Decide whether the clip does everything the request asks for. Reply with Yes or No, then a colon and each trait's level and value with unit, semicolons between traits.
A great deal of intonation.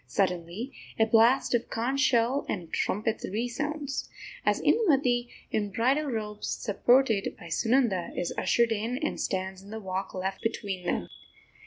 No: average, 4.6 semitones